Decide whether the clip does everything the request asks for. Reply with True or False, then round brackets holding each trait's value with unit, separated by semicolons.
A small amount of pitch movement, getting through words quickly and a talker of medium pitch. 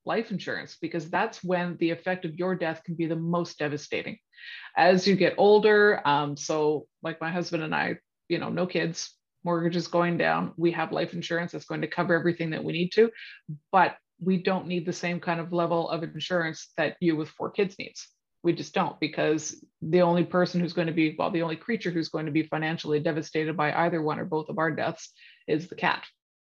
True (2.0 semitones; 215 wpm; 170 Hz)